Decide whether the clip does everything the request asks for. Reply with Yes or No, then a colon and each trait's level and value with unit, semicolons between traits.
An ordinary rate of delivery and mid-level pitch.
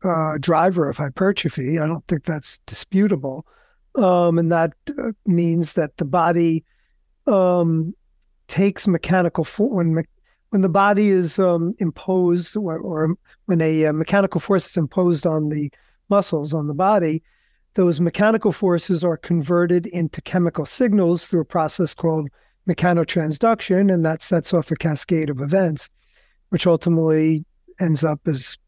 Yes: average, 145 wpm; medium, 170 Hz